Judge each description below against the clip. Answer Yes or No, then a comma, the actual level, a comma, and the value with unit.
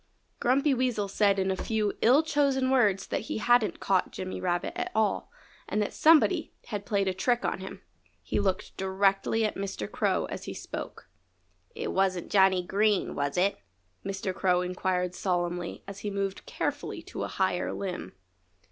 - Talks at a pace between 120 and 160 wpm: No, average, 170 wpm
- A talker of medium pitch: No, high, 195 Hz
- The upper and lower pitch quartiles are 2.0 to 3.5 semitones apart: Yes, average, 3.1 semitones